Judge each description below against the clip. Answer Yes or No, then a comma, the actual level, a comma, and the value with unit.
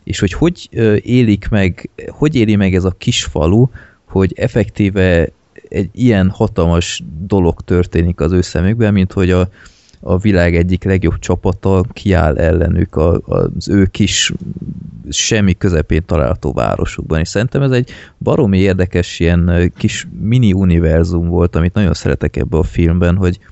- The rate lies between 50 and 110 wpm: No, average, 145 wpm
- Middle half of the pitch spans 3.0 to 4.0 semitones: Yes, average, 3.3 semitones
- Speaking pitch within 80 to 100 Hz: Yes, very low, 95 Hz